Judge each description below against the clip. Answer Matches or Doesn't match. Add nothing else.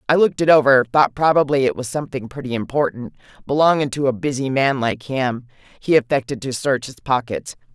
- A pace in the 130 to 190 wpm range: Matches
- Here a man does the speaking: Doesn't match